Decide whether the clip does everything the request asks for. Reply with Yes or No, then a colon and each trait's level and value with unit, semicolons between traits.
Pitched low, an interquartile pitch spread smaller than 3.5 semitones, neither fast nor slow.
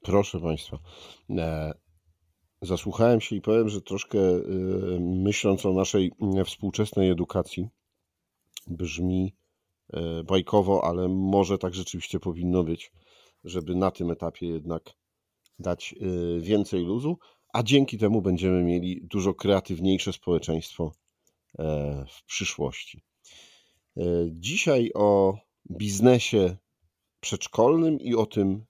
No: very low, 95 Hz; average, 2.8 semitones; slow, 95 wpm